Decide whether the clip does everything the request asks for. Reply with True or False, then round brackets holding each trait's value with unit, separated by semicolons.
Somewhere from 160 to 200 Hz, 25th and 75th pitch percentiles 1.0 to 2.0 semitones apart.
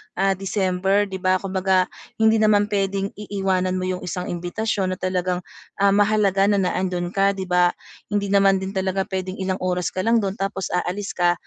True (190 Hz; 1.4 semitones)